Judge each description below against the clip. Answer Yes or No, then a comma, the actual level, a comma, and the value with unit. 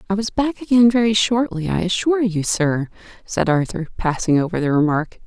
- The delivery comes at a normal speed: Yes, average, 180 wpm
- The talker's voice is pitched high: Yes, high, 195 Hz